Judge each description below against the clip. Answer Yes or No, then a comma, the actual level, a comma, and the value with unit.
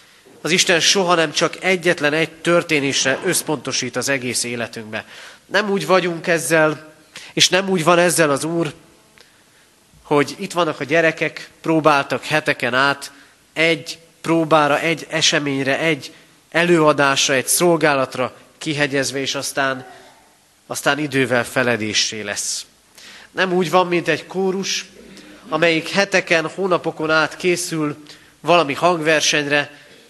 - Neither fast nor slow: Yes, average, 120 wpm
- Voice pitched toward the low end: No, medium, 155 Hz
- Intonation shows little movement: No, average, 3.2 semitones